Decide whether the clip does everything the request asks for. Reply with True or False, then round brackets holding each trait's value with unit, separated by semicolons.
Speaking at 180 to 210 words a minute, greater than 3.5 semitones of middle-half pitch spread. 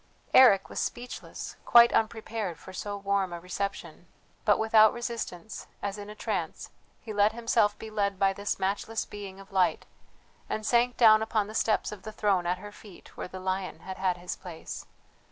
False (185 wpm; 2.5 semitones)